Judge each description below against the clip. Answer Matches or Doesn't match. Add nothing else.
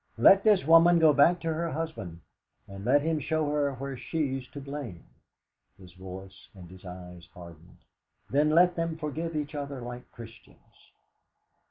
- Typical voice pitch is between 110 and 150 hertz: Matches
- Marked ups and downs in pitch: Matches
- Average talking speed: Matches